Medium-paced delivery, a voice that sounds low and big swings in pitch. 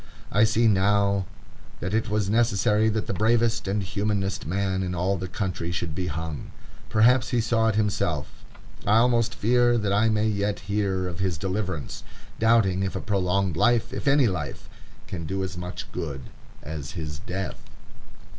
No: average, 170 wpm; low, 100 Hz; average, 3.2 semitones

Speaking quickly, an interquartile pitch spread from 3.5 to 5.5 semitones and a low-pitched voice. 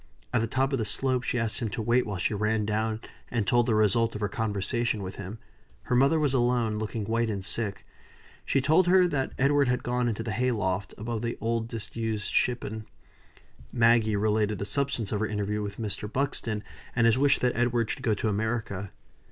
No: fast, 210 wpm; narrow, 2.6 semitones; low, 115 Hz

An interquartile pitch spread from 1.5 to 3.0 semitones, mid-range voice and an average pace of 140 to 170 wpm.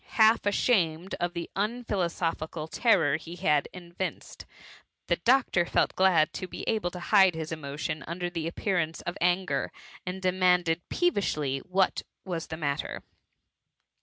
Yes: average, 2.7 semitones; medium, 175 Hz; average, 150 wpm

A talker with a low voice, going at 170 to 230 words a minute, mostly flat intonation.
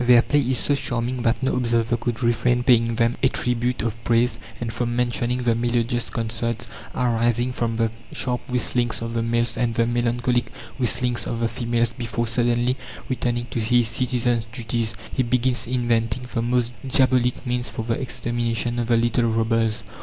Yes: low, 120 Hz; average, 175 wpm; narrow, 1.0 semitones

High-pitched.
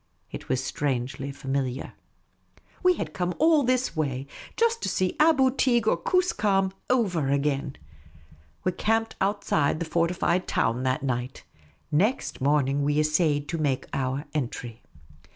No: medium, 155 Hz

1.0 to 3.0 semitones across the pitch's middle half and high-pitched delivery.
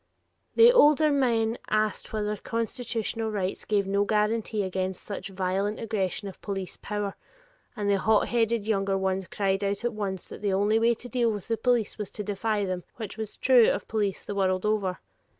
Yes: narrow, 2.5 semitones; high, 210 Hz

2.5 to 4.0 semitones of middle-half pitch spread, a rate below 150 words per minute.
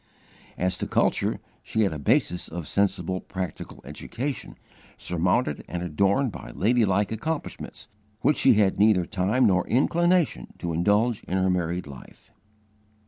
No: average, 4.4 semitones; average, 140 wpm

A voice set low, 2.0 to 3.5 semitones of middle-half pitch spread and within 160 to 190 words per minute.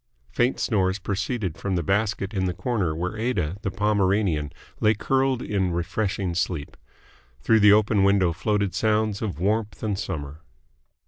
No: low, 100 Hz; average, 3.2 semitones; average, 150 wpm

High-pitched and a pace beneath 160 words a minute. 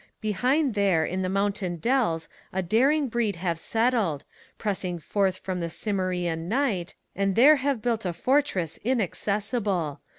Yes: high, 200 Hz; average, 140 wpm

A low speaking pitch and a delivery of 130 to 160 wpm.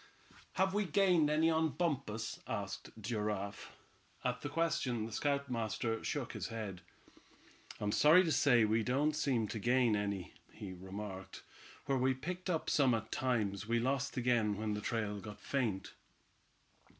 Yes: low, 120 Hz; average, 150 wpm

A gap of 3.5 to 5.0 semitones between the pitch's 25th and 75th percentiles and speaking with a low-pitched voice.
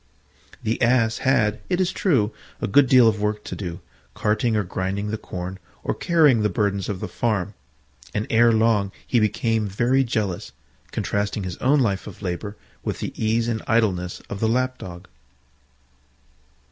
No: average, 2.8 semitones; low, 110 Hz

